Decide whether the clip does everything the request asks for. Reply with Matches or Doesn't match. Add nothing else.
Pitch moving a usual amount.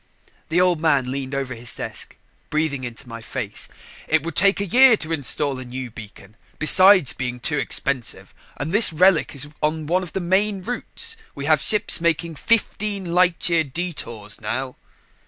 Doesn't match